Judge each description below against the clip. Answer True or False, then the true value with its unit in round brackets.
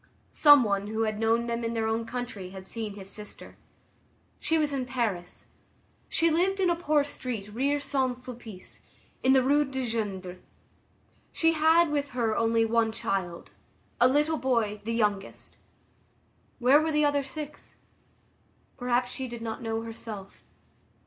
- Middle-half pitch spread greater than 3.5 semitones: True (4.4 semitones)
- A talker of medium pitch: False (235 Hz)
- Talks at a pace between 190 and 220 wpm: False (155 wpm)